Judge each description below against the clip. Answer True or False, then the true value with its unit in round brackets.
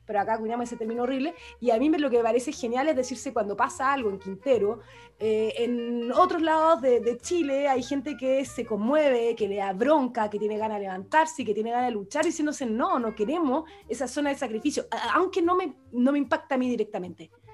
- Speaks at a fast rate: True (230 wpm)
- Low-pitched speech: False (250 Hz)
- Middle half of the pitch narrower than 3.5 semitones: False (5.0 semitones)